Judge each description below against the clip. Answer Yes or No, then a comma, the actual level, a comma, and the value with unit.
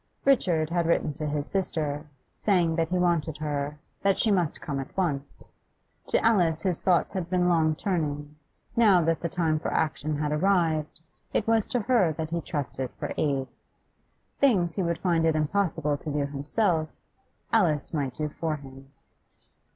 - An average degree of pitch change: Yes, average, 3.4 semitones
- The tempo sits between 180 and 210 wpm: No, average, 170 wpm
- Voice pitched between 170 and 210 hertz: No, medium, 160 Hz